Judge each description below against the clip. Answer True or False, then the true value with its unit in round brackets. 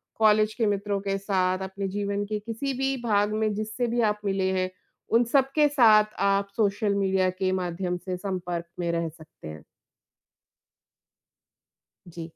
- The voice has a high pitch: True (200 Hz)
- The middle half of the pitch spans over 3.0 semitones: False (2.7 semitones)